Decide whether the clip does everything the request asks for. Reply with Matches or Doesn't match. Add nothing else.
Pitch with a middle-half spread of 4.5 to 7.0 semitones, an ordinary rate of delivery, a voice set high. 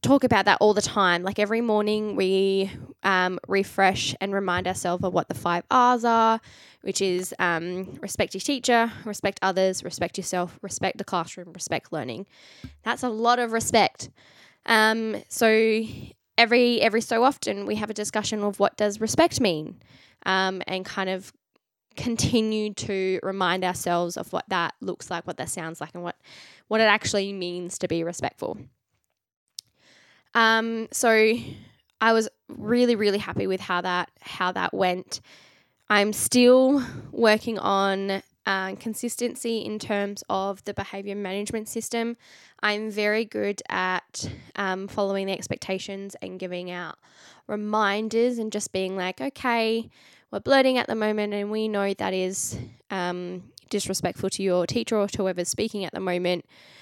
Doesn't match